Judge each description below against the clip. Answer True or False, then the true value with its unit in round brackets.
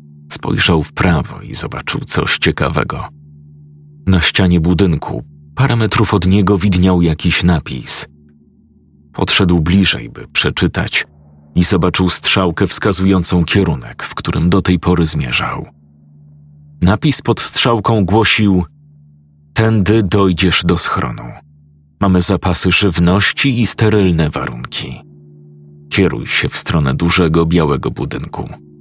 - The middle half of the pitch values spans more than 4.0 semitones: True (4.7 semitones)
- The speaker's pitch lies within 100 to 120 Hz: False (85 Hz)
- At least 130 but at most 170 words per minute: False (110 wpm)